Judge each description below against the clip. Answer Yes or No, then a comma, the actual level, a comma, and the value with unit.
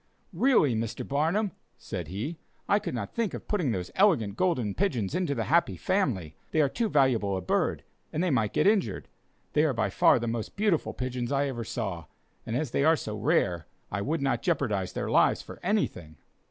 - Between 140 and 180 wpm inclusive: No, average, 200 wpm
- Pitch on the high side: No, low, 130 Hz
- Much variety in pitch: Yes, wide, 8.3 semitones